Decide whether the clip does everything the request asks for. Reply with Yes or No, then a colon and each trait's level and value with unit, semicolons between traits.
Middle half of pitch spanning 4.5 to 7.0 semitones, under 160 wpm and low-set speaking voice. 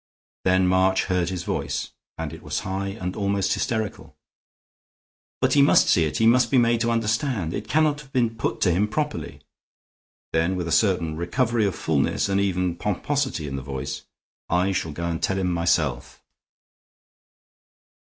No: average, 4.9 semitones; average, 170 wpm; very low, 95 Hz